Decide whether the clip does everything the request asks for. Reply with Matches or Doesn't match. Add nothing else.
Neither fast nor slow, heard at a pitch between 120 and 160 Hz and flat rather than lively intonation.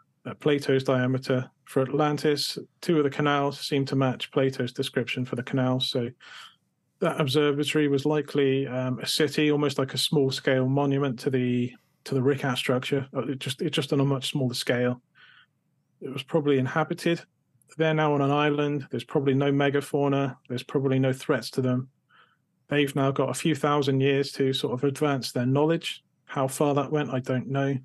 Matches